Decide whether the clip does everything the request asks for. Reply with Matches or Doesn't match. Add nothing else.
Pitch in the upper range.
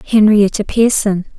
Matches